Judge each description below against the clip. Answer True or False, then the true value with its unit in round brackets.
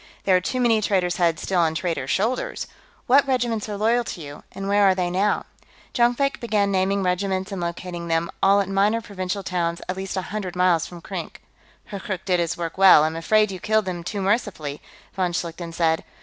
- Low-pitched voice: False (190 Hz)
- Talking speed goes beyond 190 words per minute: True (205 wpm)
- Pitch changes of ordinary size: True (3.1 semitones)